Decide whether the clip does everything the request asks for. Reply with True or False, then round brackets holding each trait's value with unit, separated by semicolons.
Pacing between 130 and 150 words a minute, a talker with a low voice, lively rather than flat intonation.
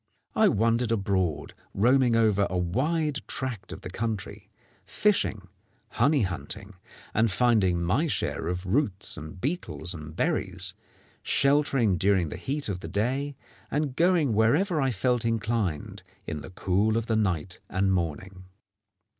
True (140 wpm; 110 Hz; 5.9 semitones)